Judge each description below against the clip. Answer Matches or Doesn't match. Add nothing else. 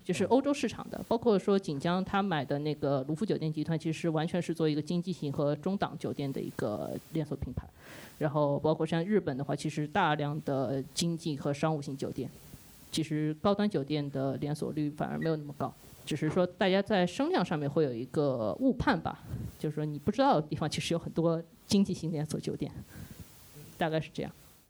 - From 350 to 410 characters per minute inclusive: Doesn't match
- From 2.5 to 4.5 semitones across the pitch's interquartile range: Matches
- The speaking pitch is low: Doesn't match